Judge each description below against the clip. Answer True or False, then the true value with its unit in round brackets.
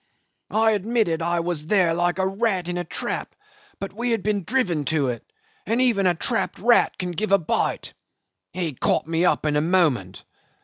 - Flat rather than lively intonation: False (4.4 semitones)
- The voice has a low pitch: False (180 Hz)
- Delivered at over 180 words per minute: True (190 wpm)